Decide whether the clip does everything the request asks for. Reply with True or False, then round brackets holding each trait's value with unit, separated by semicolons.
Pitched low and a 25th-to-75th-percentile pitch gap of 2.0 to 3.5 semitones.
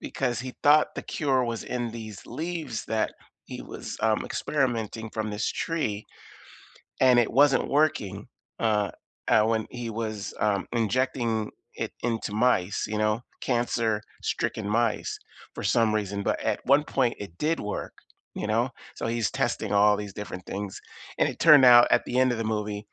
True (115 Hz; 3.0 semitones)